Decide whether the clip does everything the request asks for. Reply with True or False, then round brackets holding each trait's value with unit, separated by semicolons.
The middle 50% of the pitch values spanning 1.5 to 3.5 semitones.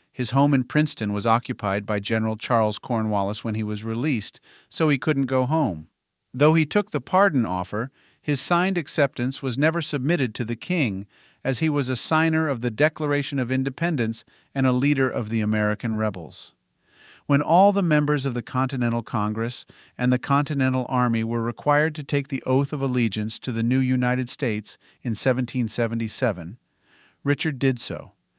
False (4.3 semitones)